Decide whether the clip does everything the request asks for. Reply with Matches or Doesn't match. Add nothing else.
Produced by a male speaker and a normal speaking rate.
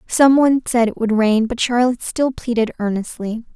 Doesn't match